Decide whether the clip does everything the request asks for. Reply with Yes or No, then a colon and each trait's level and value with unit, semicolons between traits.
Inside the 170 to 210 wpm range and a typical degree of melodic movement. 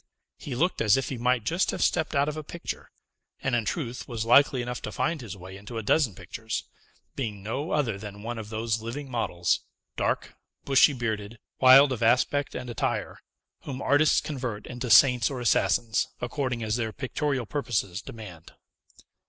Yes: average, 175 wpm; average, 3.8 semitones